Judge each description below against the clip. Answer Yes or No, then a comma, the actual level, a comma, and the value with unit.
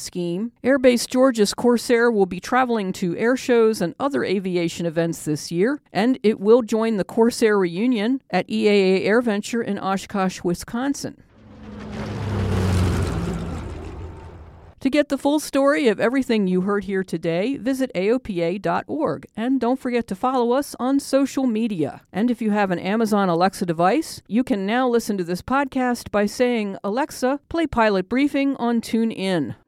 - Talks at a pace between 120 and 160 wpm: Yes, average, 150 wpm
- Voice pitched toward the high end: Yes, high, 220 Hz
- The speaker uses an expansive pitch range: Yes, wide, 5.7 semitones